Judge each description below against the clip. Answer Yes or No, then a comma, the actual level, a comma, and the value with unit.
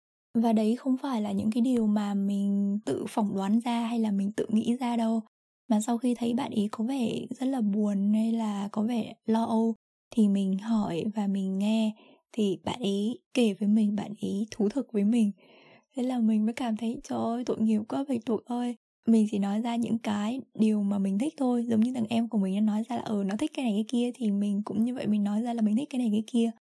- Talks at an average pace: No, fast, 255 wpm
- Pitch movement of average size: No, narrow, 2.2 semitones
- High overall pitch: Yes, high, 220 Hz